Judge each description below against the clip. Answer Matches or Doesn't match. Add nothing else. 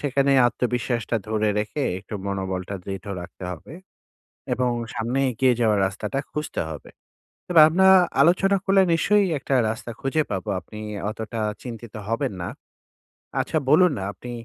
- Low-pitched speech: Matches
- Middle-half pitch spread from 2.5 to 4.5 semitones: Doesn't match